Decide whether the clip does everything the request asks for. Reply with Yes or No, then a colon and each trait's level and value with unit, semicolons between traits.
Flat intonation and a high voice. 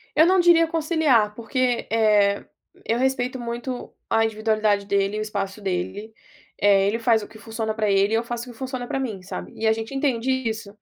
No: average, 3.3 semitones; high, 225 Hz